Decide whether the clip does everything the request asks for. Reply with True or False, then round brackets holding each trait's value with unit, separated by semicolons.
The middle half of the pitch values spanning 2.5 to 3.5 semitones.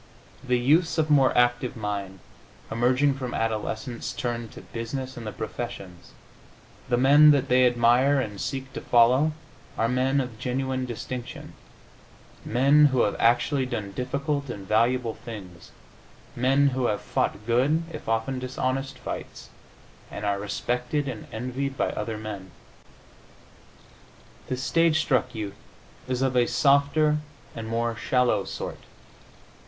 True (3.0 semitones)